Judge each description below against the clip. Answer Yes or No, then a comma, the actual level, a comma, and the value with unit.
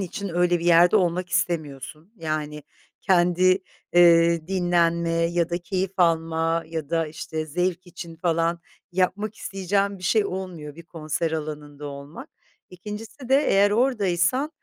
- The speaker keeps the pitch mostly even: Yes, narrow, 2.3 semitones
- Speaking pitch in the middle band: Yes, medium, 175 Hz